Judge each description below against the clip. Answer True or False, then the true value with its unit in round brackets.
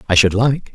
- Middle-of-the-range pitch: False (115 Hz)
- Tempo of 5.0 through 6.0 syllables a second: True (5.5 syllables/s)